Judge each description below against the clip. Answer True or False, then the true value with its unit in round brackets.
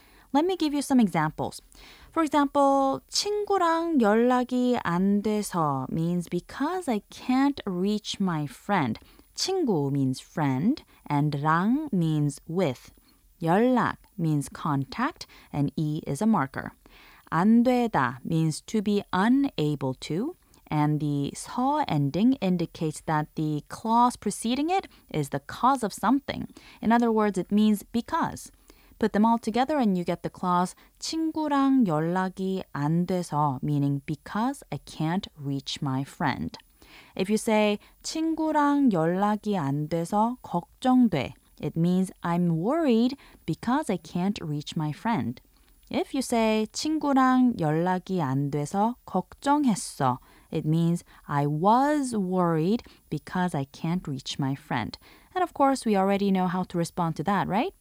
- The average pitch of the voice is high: True (195 Hz)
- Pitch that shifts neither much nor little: False (8.0 semitones)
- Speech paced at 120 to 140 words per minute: True (135 wpm)